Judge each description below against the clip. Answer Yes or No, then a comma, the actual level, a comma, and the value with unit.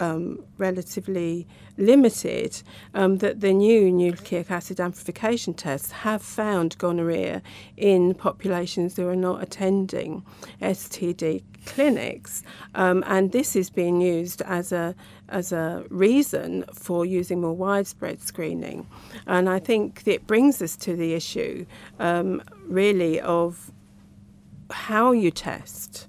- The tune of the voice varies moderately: No, narrow, 2.3 semitones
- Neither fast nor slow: No, slow, 125 wpm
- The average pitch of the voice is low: No, medium, 180 Hz